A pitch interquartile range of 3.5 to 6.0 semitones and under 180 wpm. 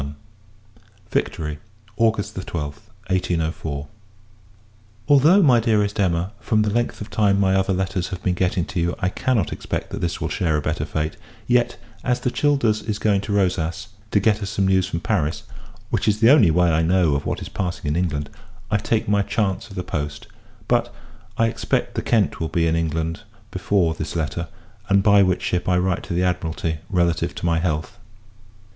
No: average, 3.9 semitones; average, 195 wpm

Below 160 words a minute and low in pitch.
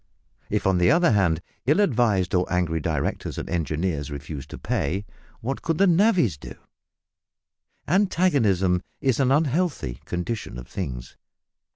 Yes: slow, 135 wpm; very low, 95 Hz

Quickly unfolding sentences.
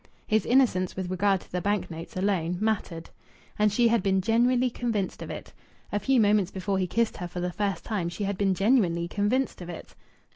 Yes: fast, 210 wpm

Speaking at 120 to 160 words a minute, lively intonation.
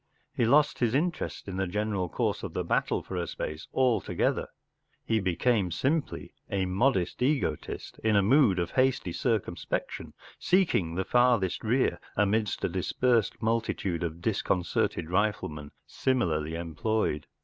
Yes: average, 140 wpm; wide, 5.9 semitones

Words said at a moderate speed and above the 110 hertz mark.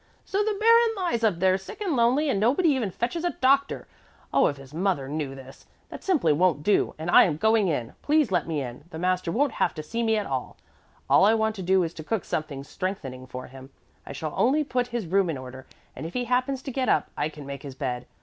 No: fast, 245 wpm; high, 190 Hz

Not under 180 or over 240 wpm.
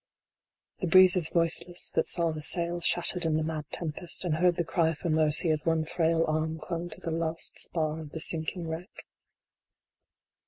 Yes: average, 185 wpm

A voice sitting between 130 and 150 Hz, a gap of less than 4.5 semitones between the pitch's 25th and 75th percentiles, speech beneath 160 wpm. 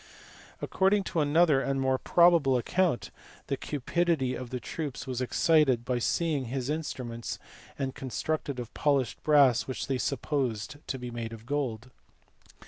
Yes: low, 135 Hz; average, 3.5 semitones; average, 140 wpm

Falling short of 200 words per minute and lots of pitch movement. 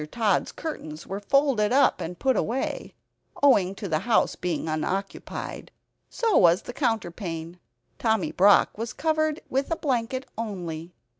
Yes: average, 140 wpm; wide, 6.8 semitones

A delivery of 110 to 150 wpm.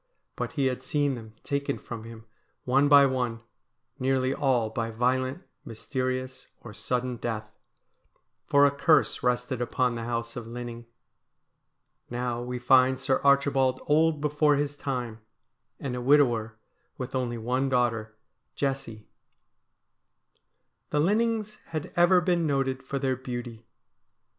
Yes: slow, 135 wpm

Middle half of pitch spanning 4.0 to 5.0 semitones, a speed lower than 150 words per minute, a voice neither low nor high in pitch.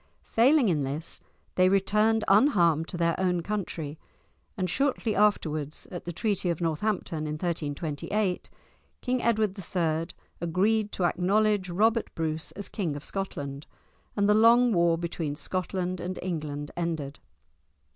Yes: average, 4.6 semitones; slow, 135 wpm; medium, 180 Hz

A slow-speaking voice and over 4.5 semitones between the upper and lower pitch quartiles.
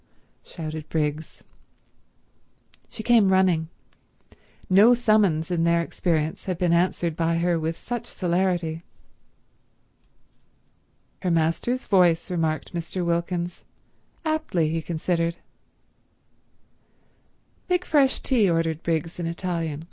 No: slow, 100 wpm; narrow, 2.5 semitones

